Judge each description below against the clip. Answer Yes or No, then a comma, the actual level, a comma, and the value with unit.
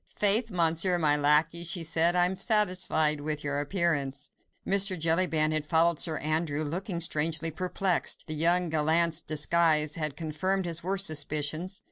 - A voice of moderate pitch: Yes, medium, 165 Hz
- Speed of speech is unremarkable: Yes, average, 150 wpm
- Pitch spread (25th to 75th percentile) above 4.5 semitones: No, average, 2.7 semitones